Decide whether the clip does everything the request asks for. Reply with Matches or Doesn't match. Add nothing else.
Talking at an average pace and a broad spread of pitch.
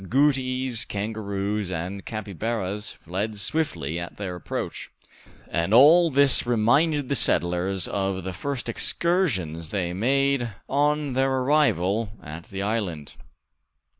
Doesn't match